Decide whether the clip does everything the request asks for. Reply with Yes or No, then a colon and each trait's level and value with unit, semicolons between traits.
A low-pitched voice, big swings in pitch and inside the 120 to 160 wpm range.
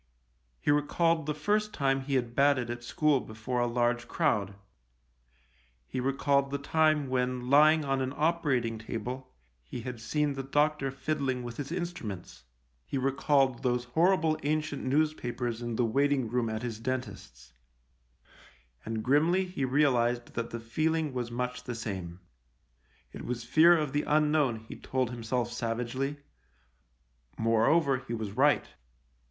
No: low, 130 Hz; average, 3.8 semitones; average, 145 wpm